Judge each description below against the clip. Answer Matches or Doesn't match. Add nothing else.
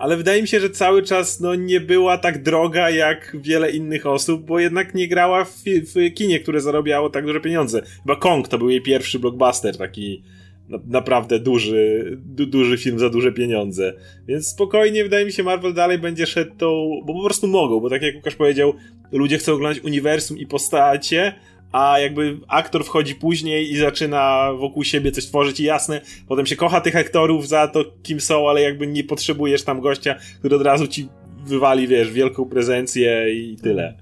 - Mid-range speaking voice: Matches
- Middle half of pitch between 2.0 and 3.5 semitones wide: Doesn't match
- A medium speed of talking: Doesn't match